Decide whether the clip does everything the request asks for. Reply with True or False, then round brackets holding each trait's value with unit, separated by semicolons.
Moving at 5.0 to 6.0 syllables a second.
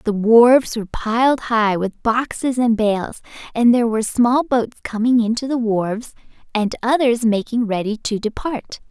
False (4.7 syllables/s)